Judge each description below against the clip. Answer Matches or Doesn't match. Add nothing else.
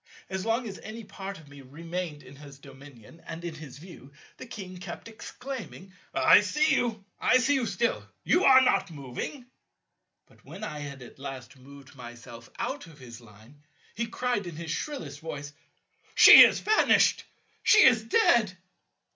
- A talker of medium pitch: Matches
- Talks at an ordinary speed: Matches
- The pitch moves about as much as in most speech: Doesn't match